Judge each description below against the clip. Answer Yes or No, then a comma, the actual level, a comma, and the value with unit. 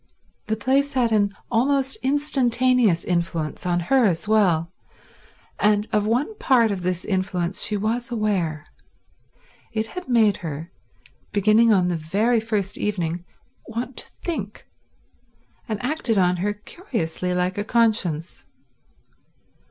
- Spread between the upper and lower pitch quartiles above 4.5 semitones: Yes, average, 4.9 semitones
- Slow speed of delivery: Yes, slow, 130 wpm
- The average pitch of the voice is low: No, high, 210 Hz